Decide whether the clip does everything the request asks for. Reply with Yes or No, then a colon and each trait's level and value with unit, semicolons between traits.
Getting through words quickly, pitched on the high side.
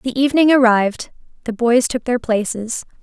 No: average, 160 wpm; high, 240 Hz